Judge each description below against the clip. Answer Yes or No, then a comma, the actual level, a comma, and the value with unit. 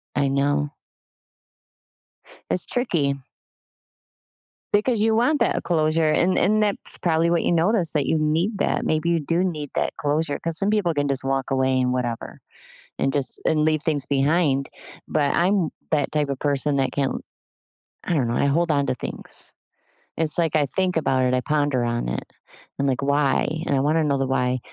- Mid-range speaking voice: Yes, medium, 150 Hz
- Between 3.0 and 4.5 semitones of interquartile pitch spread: Yes, average, 3.6 semitones